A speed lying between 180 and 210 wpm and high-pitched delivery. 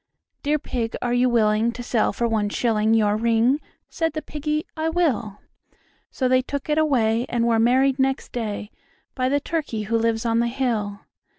Yes: average, 185 wpm; high, 240 Hz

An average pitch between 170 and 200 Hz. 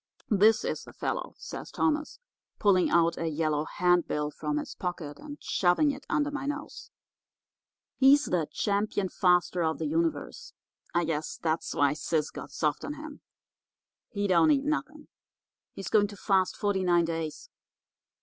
Yes: medium, 185 Hz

